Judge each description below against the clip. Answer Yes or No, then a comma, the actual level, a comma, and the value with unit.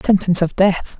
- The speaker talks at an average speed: Yes, average, 180 wpm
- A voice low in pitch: No, medium, 185 Hz